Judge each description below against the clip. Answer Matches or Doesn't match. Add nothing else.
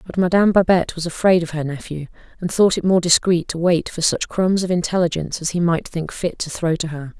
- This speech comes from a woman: Matches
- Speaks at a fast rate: Matches